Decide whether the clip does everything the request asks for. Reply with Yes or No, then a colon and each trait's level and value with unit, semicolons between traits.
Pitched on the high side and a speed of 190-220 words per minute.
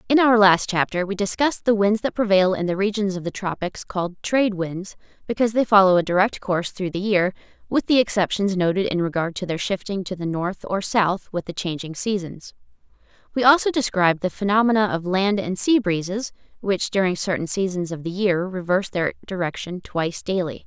Yes: high, 195 Hz; average, 195 wpm